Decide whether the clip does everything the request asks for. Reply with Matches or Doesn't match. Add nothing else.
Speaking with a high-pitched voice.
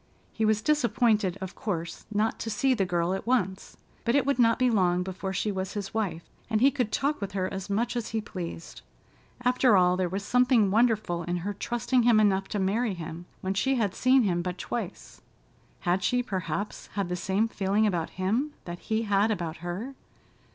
Matches